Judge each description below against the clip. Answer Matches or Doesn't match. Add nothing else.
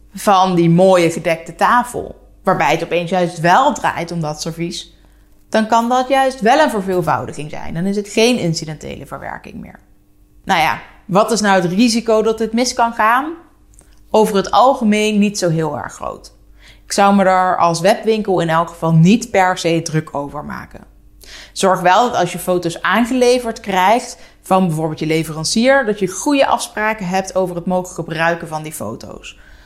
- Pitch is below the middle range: Doesn't match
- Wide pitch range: Doesn't match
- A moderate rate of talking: Matches